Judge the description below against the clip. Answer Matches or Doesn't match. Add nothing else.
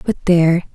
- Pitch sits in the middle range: Matches